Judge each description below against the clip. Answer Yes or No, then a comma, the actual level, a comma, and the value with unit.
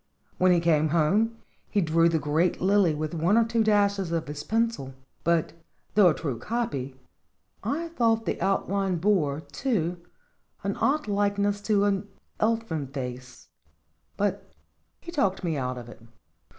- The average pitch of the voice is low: No, medium, 185 Hz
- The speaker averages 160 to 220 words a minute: No, average, 150 wpm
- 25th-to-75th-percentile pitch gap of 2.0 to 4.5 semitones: No, average, 5.2 semitones